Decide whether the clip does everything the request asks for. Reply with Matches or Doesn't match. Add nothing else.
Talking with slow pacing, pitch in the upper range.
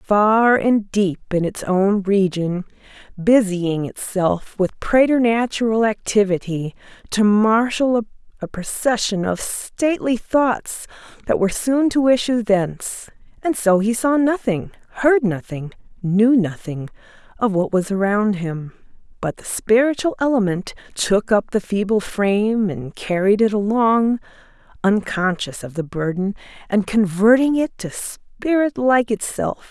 Matches